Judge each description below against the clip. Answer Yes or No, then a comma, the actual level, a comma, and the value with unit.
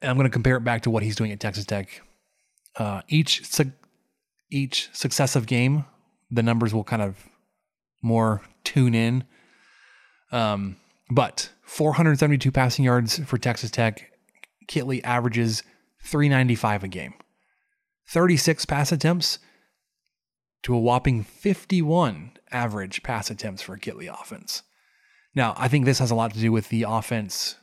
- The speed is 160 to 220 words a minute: No, average, 145 wpm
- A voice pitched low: Yes, low, 125 Hz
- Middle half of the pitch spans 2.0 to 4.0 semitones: No, average, 4.6 semitones